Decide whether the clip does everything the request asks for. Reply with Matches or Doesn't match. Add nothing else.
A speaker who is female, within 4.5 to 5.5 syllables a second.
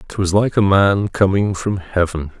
Doesn't match